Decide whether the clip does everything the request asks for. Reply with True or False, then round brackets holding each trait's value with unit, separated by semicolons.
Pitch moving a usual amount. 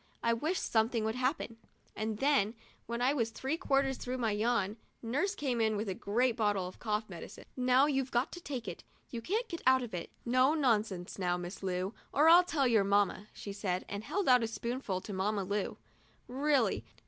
True (4.5 semitones)